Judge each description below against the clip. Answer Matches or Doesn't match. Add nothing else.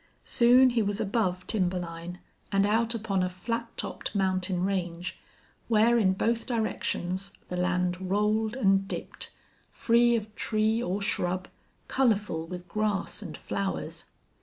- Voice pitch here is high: Matches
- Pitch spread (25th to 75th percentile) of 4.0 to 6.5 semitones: Doesn't match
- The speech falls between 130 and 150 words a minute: Matches